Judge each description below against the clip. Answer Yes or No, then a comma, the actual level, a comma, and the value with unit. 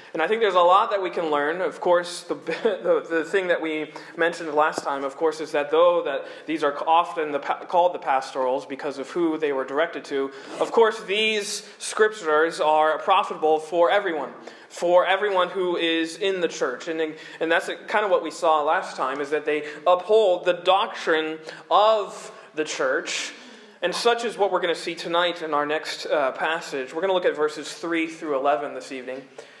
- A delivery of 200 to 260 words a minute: Yes, fast, 205 wpm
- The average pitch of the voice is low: No, medium, 170 Hz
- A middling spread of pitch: Yes, average, 4.8 semitones